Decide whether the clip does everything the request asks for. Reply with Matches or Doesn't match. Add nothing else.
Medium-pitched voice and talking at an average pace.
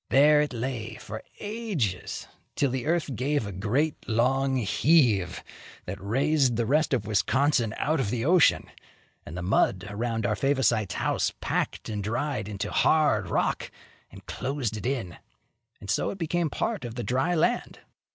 Doesn't match